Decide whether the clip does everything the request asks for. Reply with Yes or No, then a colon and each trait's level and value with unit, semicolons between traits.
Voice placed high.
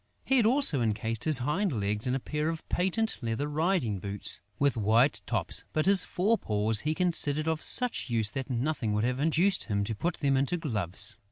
No: medium, 140 Hz